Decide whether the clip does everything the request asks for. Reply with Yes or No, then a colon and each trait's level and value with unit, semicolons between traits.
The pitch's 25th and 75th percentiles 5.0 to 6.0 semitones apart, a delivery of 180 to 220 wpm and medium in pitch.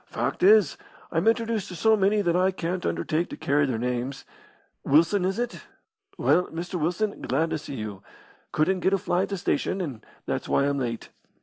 Yes: average, 5.3 semitones; average, 195 wpm; medium, 175 Hz